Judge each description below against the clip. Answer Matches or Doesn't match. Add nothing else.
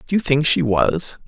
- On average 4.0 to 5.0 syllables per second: Matches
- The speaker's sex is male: Matches